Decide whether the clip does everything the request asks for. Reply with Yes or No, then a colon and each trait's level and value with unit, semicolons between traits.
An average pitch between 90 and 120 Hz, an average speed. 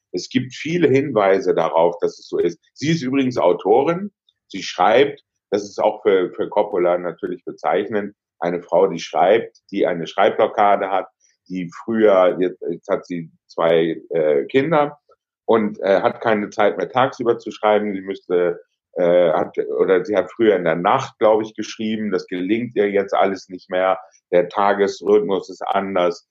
Yes: low, 110 Hz; average, 165 wpm